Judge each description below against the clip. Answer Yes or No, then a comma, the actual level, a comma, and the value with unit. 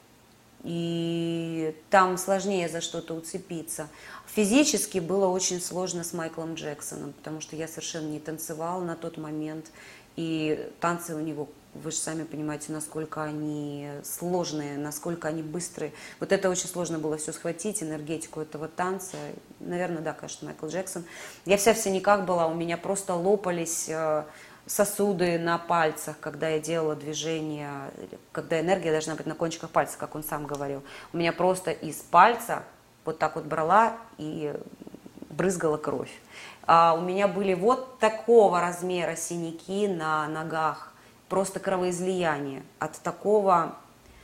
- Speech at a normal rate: Yes, average, 140 wpm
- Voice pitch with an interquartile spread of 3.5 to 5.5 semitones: No, average, 2.8 semitones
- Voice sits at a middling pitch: Yes, medium, 165 Hz